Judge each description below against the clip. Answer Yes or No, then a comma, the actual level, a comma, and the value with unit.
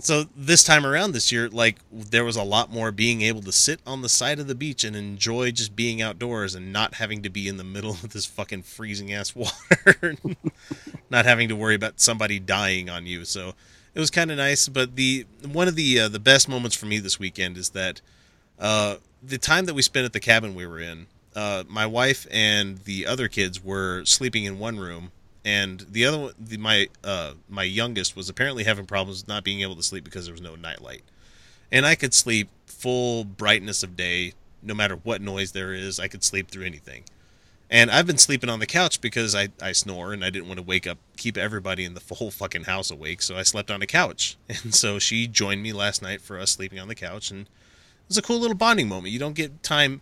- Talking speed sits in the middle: No, fast, 235 wpm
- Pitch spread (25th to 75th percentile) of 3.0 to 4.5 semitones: Yes, average, 4.1 semitones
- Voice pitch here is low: Yes, low, 105 Hz